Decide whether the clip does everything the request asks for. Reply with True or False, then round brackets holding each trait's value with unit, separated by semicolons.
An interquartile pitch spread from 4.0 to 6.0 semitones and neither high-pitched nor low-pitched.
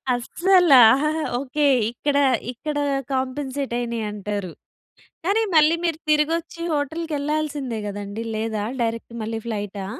False (5.3 semitones; 265 Hz)